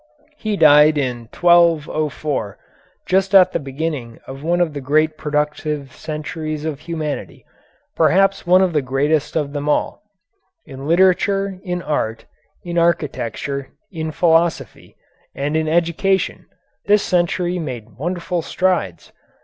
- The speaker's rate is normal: No, slow, 125 wpm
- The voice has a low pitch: No, medium, 155 Hz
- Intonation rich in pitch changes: No, average, 3.4 semitones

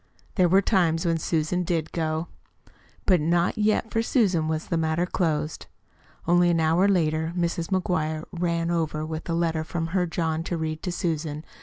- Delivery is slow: No, average, 175 wpm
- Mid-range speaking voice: Yes, medium, 165 Hz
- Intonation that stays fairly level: Yes, narrow, 2.0 semitones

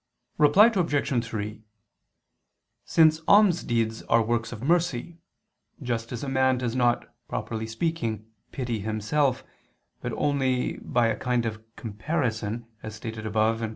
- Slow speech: Yes, slow, 130 wpm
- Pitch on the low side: Yes, low, 120 Hz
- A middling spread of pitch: Yes, average, 4.4 semitones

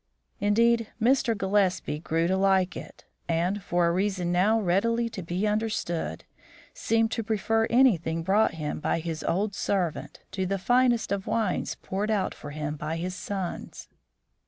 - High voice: Yes, high, 195 Hz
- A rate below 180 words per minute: Yes, average, 155 wpm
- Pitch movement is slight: No, average, 4.2 semitones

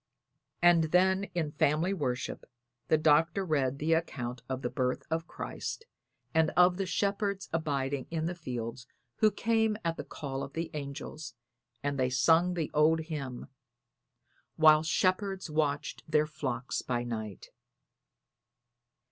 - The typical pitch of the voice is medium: Yes, medium, 155 Hz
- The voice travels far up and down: No, average, 4.3 semitones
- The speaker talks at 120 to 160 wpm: Yes, average, 140 wpm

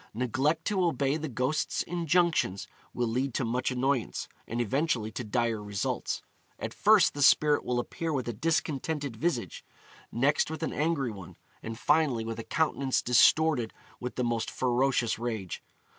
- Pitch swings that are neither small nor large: Yes, average, 5.0 semitones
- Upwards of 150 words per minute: Yes, average, 160 wpm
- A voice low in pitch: Yes, low, 130 Hz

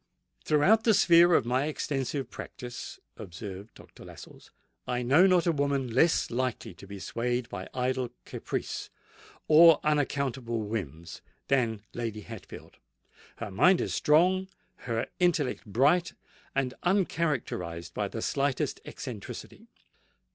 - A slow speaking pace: Yes, slow, 120 wpm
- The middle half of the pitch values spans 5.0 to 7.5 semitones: Yes, wide, 5.5 semitones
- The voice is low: Yes, low, 130 Hz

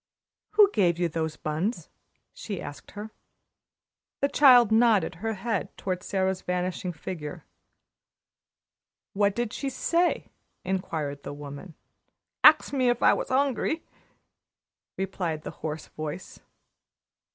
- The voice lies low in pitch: No, high, 190 Hz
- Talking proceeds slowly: Yes, slow, 120 wpm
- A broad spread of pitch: Yes, wide, 6.4 semitones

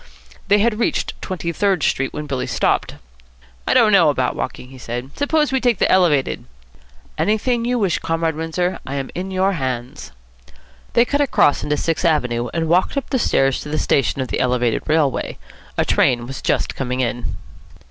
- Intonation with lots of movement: Yes, wide, 7.1 semitones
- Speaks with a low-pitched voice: No, medium, 160 Hz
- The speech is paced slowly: No, average, 185 wpm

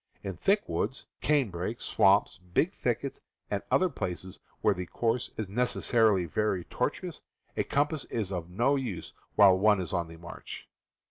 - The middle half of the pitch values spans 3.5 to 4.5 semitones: No, average, 5.2 semitones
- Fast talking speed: No, average, 155 wpm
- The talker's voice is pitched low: Yes, low, 100 Hz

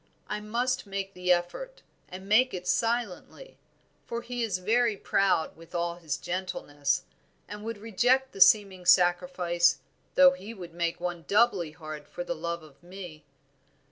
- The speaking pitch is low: No, medium, 185 Hz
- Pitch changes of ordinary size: Yes, average, 4.6 semitones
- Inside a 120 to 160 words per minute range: Yes, average, 150 wpm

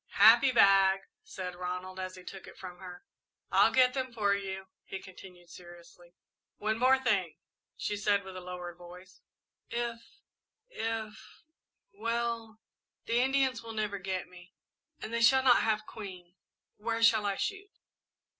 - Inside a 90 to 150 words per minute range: Yes, average, 145 wpm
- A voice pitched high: Yes, high, 200 Hz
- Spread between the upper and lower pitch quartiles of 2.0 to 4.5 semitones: Yes, average, 3.9 semitones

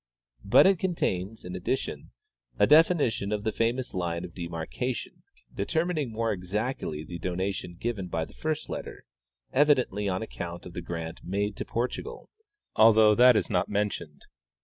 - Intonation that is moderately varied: No, wide, 5.8 semitones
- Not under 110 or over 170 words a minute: Yes, average, 160 wpm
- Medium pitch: No, low, 105 Hz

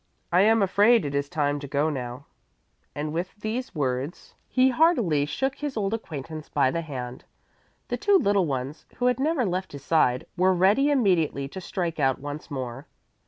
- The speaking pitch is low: No, medium, 165 Hz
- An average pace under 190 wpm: Yes, average, 180 wpm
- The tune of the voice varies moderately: No, wide, 7.3 semitones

